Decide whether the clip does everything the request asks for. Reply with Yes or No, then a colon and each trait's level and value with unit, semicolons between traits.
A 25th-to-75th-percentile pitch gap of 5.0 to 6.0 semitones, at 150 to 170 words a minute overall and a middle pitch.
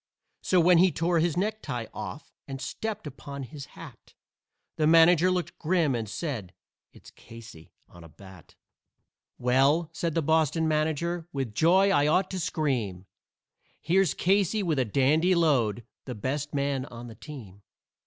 Yes: wide, 5.4 semitones; average, 155 wpm; medium, 150 Hz